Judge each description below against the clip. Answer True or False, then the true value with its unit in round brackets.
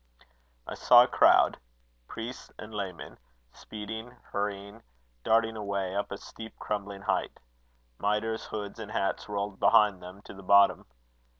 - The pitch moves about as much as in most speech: False (1.9 semitones)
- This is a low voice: True (105 Hz)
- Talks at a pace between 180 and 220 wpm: False (135 wpm)